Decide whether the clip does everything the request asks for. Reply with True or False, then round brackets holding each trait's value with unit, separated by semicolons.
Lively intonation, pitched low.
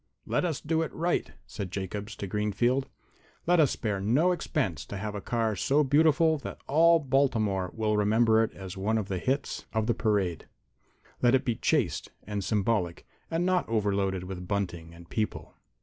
True (5.9 semitones; 110 Hz)